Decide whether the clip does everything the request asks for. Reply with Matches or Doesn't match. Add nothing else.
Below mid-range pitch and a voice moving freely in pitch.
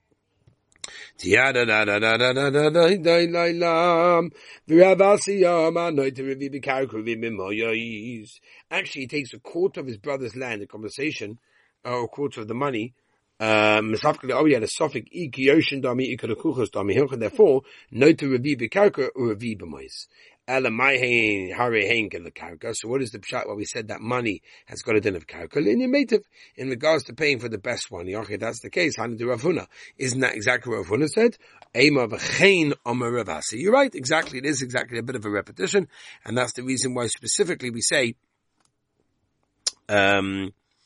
Matches